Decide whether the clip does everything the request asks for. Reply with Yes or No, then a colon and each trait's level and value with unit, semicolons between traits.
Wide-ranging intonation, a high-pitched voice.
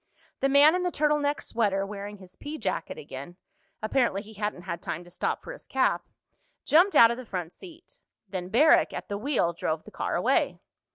Yes: wide, 8.1 semitones; high, 210 Hz